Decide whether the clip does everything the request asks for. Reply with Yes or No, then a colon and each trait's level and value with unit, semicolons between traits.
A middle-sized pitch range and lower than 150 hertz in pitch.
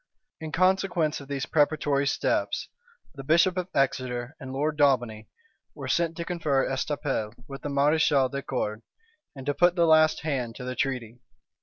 Yes: average, 3.3 semitones; medium, 140 Hz